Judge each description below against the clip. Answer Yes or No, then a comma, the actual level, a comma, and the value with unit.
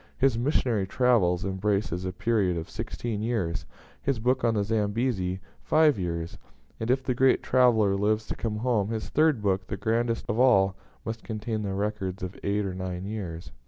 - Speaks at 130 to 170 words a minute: No, average, 180 wpm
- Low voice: Yes, low, 105 Hz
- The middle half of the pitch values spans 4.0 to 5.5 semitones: No, average, 3.6 semitones